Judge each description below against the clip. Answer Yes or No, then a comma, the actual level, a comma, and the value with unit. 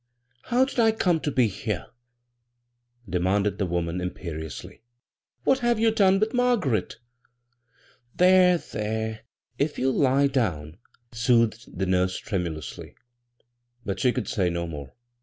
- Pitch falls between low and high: No, low, 110 Hz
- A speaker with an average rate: No, slow, 130 wpm